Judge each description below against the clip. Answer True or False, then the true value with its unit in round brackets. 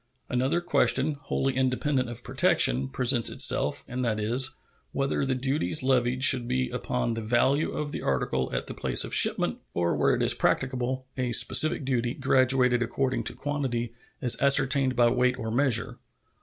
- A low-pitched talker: True (125 Hz)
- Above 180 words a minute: False (170 wpm)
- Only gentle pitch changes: True (2.1 semitones)